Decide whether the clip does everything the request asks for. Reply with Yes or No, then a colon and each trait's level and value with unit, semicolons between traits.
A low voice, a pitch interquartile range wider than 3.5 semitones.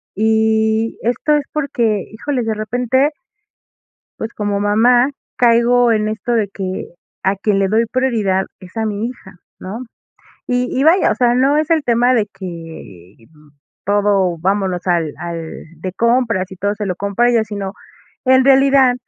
No: high, 220 Hz; average, 4.2 semitones